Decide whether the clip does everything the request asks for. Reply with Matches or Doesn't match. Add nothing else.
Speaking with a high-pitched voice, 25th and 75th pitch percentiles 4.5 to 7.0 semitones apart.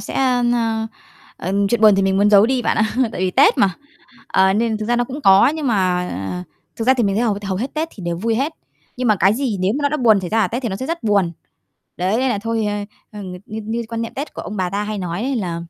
Doesn't match